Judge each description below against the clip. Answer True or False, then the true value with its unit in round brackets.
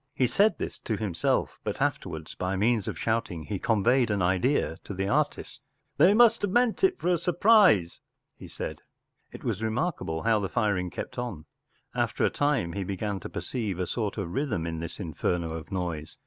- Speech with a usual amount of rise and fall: False (6.8 semitones)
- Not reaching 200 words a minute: False (205 wpm)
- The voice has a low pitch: True (105 Hz)